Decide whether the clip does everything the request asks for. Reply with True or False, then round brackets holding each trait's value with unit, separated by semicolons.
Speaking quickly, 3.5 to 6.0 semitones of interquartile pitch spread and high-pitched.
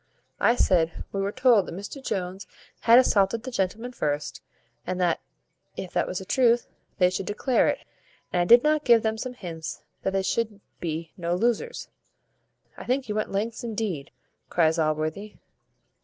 False (170 wpm; 4.8 semitones; 200 Hz)